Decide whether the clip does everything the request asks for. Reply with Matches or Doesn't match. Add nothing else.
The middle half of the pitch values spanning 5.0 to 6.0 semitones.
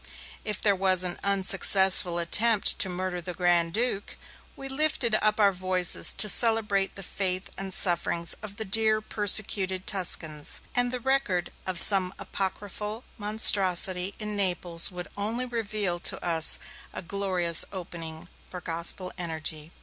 Doesn't match